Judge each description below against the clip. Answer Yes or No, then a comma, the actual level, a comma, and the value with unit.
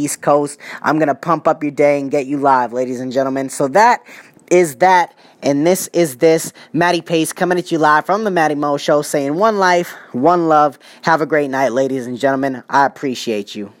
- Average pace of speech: No, fast, 215 wpm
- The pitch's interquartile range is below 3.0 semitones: No, average, 3.6 semitones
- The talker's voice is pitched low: No, medium, 150 Hz